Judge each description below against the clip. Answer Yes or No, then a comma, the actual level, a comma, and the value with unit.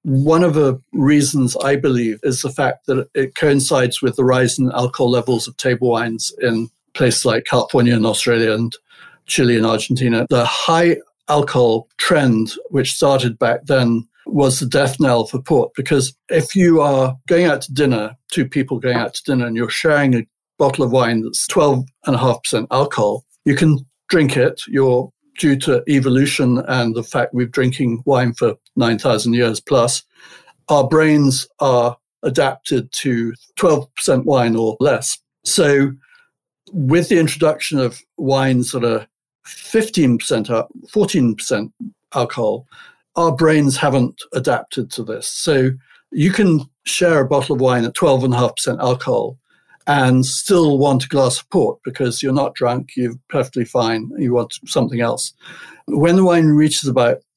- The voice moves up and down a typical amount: Yes, average, 3.1 semitones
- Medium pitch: No, low, 130 Hz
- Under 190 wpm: Yes, average, 155 wpm